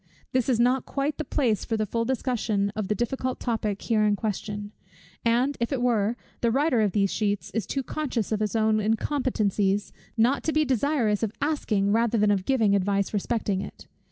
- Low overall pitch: No, high, 225 Hz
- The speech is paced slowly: No, average, 195 wpm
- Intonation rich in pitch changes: No, average, 3.6 semitones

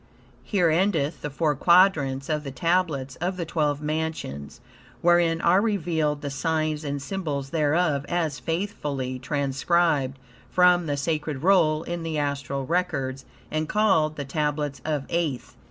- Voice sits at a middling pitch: Yes, medium, 155 Hz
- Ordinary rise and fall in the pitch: Yes, average, 3.4 semitones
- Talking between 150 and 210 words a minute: No, average, 140 wpm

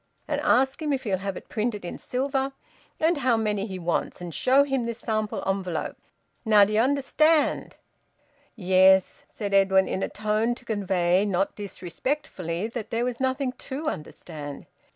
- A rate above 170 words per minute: No, average, 160 wpm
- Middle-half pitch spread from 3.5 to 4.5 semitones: No, average, 5.3 semitones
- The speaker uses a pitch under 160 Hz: No, high, 215 Hz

